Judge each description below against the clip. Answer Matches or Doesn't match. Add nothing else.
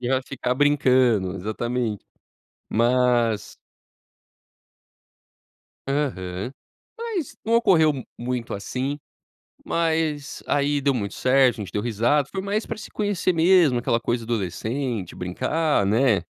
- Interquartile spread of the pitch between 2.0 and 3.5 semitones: Doesn't match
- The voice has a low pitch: Matches